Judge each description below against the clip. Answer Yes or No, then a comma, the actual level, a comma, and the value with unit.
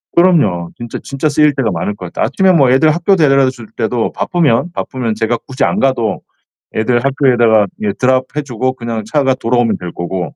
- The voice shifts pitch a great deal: No, average, 4.1 semitones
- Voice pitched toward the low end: Yes, low, 130 Hz